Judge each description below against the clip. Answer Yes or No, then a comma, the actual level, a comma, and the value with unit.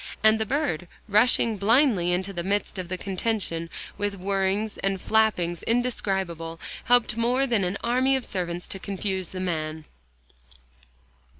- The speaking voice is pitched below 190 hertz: No, high, 195 Hz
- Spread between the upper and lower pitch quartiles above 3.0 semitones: Yes, average, 3.9 semitones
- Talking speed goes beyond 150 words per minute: No, average, 140 wpm